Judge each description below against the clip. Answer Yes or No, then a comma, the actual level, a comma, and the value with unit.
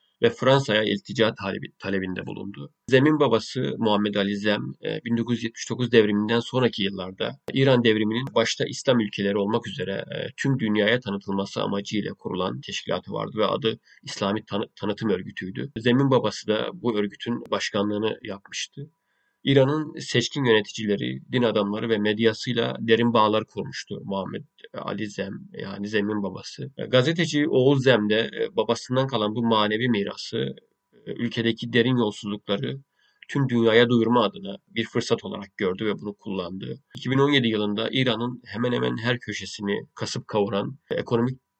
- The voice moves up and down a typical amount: Yes, average, 3.4 semitones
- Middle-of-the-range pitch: No, low, 115 Hz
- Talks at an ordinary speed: Yes, average, 130 wpm